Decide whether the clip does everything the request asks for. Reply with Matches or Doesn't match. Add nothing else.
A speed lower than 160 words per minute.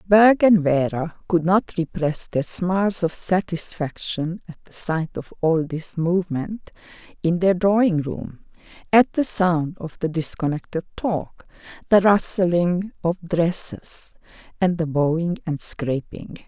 Matches